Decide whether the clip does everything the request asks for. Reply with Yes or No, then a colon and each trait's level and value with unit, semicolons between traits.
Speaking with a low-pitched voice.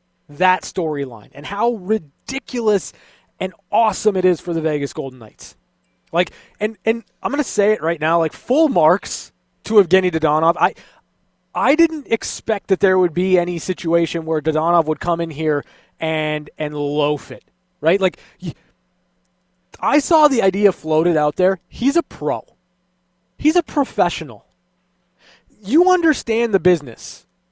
No: medium, 185 Hz